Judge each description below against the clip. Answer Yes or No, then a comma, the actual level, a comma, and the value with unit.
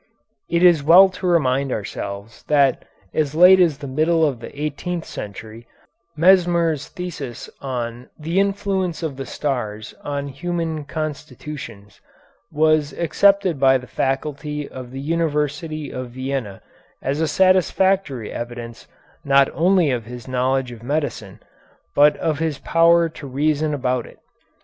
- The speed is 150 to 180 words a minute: No, slow, 135 wpm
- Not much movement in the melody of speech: No, average, 4.4 semitones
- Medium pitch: Yes, medium, 145 Hz